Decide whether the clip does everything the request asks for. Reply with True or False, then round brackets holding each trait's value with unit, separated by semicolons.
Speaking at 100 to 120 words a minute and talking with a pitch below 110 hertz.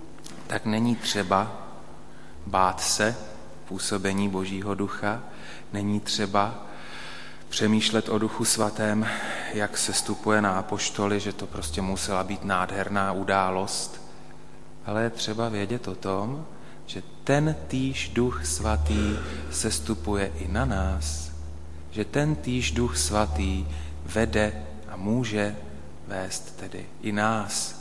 True (115 wpm; 100 Hz)